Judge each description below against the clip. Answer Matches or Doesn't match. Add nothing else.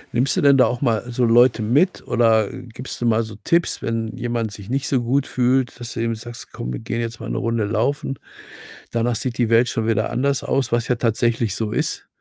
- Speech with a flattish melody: Matches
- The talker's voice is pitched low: Matches